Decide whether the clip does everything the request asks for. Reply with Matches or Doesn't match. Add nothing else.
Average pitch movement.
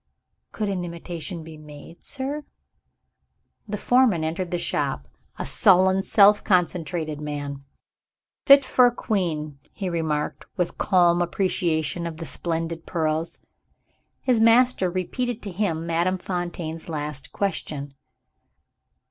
Matches